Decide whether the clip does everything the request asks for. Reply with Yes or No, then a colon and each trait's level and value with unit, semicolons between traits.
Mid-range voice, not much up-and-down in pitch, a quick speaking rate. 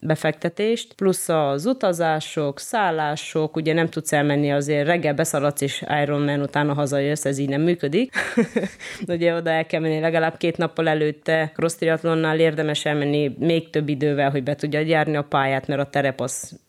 Yes: medium, 155 Hz; narrow, 2.2 semitones; fast, 165 wpm